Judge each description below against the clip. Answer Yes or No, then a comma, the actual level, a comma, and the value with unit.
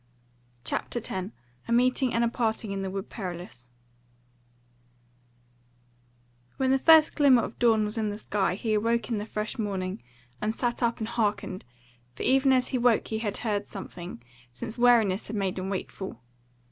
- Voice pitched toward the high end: Yes, high, 220 Hz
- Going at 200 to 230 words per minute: No, average, 170 wpm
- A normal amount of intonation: Yes, average, 3.4 semitones